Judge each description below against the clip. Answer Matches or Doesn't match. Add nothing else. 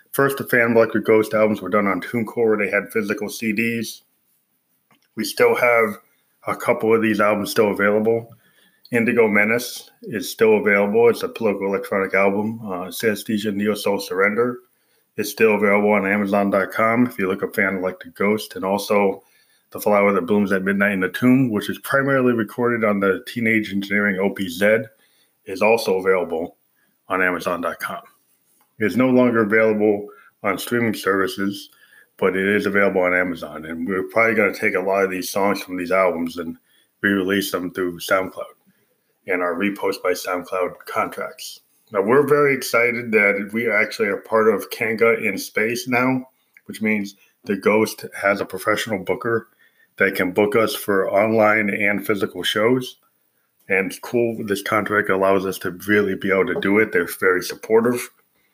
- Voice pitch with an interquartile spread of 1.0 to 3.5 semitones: Matches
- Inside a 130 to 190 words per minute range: Matches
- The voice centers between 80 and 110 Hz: Matches